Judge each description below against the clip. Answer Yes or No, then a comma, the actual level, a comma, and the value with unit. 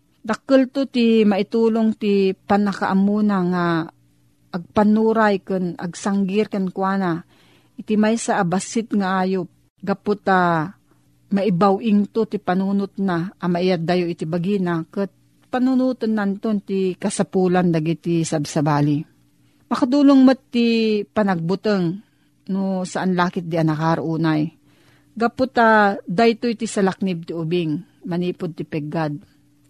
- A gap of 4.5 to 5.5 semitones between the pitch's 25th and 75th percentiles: No, average, 3.8 semitones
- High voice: Yes, high, 195 Hz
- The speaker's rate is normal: No, slow, 105 wpm